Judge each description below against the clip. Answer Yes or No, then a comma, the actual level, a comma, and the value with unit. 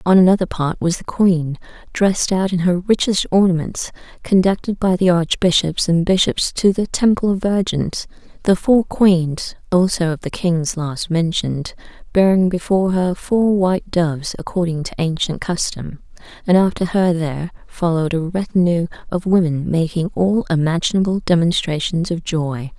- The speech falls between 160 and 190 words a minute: No, average, 150 wpm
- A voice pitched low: No, medium, 175 Hz